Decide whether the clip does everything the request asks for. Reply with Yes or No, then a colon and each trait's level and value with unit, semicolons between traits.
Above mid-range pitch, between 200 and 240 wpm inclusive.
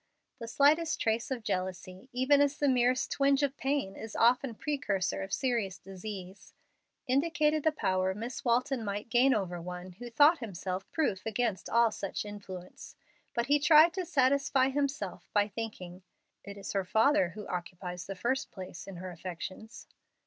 No: high, 225 Hz; average, 165 wpm